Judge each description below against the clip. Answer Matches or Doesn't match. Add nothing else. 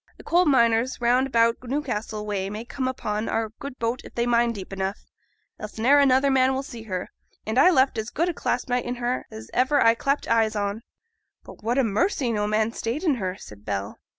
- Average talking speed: Doesn't match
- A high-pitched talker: Matches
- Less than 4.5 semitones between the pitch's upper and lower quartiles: Matches